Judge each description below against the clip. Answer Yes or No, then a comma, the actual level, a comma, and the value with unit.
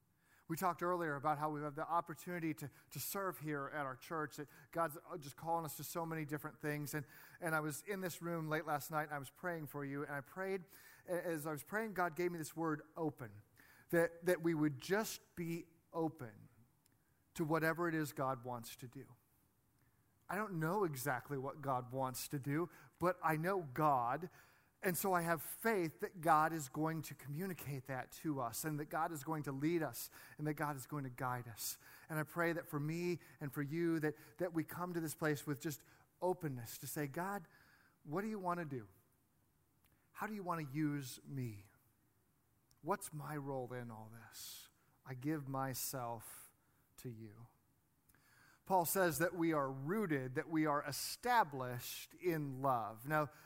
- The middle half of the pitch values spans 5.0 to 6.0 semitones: No, average, 3.8 semitones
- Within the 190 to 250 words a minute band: Yes, average, 195 wpm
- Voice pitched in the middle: Yes, medium, 150 Hz